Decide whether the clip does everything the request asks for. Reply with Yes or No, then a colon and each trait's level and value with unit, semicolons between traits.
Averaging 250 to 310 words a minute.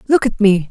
Yes: fast, 255 wpm